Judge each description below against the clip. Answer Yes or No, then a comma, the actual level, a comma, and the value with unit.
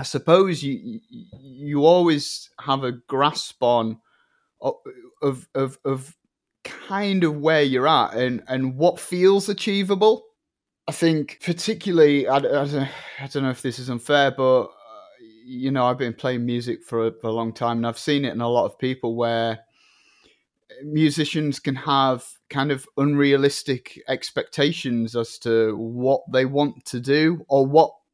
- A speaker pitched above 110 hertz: Yes, medium, 140 Hz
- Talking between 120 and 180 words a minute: Yes, average, 150 wpm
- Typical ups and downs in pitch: Yes, average, 4.5 semitones